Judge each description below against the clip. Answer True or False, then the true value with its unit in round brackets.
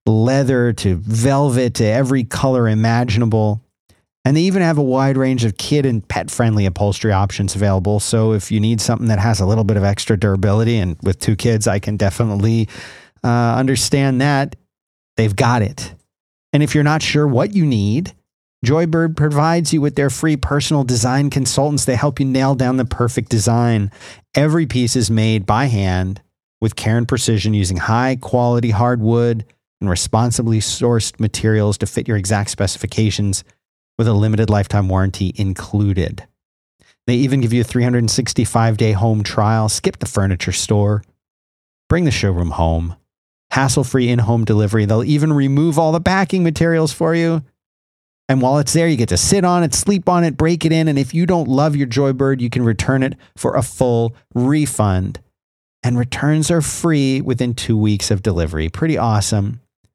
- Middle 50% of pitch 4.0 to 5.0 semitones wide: True (4.7 semitones)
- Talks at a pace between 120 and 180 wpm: True (175 wpm)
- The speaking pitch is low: True (115 Hz)